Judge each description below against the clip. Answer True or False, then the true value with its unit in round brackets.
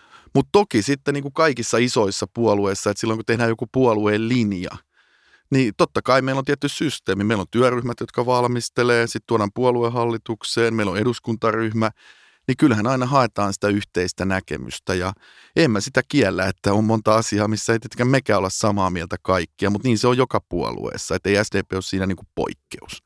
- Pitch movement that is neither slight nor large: True (3.6 semitones)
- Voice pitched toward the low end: True (115 Hz)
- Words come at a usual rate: False (180 wpm)